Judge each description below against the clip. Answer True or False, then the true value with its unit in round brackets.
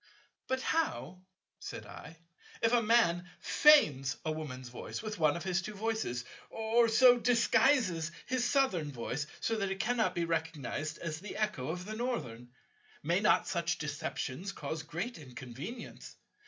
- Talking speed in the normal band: True (150 wpm)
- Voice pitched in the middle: True (180 Hz)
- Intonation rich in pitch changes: True (7.0 semitones)